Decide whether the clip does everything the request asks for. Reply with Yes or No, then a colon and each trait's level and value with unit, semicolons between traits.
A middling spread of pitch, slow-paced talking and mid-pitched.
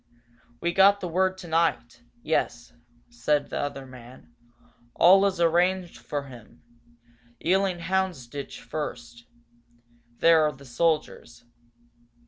No: wide, 6.7 semitones; slow, 110 wpm; medium, 155 Hz